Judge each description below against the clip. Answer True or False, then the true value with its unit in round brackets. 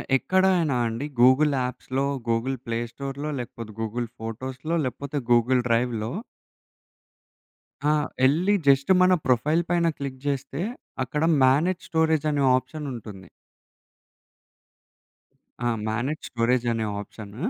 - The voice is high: False (130 Hz)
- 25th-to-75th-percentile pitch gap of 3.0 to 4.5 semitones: True (4.2 semitones)